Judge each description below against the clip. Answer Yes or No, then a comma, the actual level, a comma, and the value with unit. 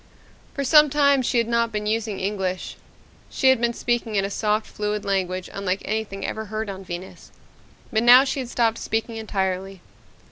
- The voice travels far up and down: No, average, 3.2 semitones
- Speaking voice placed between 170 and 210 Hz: No, high, 220 Hz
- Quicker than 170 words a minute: Yes, average, 180 wpm